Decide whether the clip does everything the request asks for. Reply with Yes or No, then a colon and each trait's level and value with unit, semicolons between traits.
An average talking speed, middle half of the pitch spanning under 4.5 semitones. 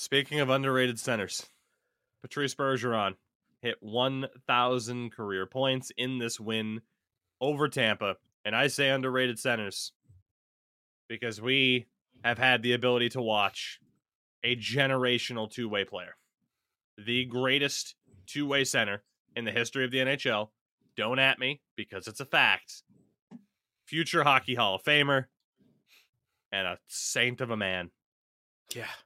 No: slow, 130 wpm; average, 3.0 semitones